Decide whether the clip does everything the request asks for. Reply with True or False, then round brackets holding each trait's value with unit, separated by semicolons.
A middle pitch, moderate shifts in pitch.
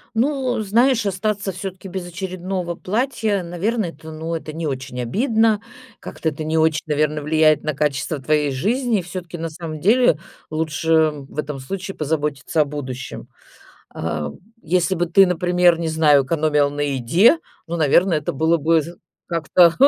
True (165 Hz; 3.9 semitones)